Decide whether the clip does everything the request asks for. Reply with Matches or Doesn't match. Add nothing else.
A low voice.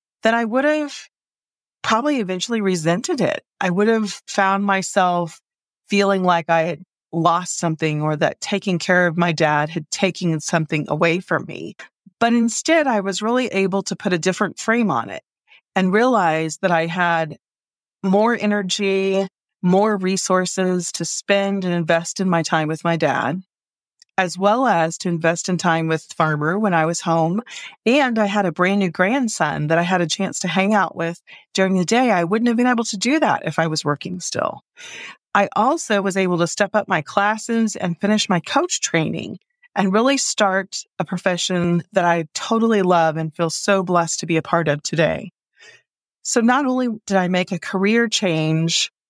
Doesn't match